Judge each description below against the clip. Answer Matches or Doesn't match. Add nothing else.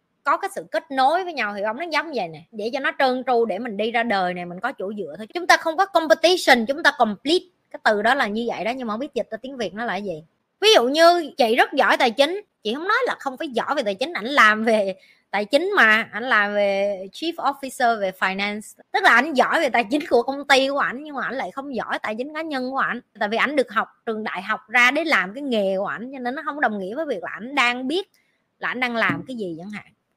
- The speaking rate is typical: Doesn't match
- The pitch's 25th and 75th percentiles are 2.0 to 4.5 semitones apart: Doesn't match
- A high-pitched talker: Matches